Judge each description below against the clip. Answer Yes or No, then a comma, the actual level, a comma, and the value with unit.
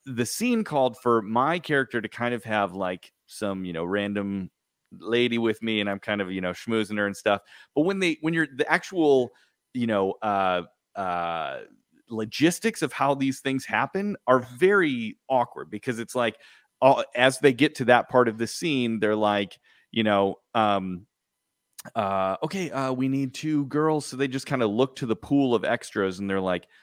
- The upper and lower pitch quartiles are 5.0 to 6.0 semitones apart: Yes, wide, 5.4 semitones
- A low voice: Yes, low, 120 Hz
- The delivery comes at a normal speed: Yes, average, 195 wpm